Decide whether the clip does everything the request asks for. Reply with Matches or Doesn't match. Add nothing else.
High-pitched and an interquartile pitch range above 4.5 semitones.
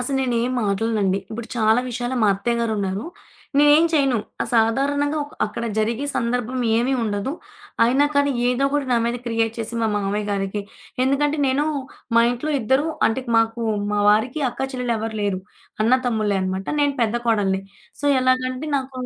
Doesn't match